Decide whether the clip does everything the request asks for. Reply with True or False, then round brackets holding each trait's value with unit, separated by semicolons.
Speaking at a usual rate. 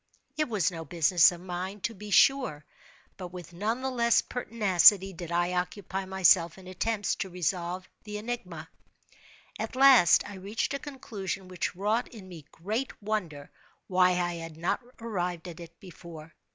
True (165 wpm)